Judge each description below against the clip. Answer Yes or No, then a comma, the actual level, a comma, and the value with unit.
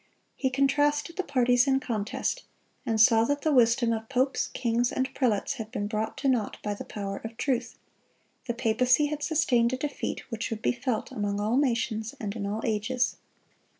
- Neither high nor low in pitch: No, high, 240 Hz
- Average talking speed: Yes, average, 185 wpm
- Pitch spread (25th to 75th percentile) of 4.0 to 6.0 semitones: No, average, 3.3 semitones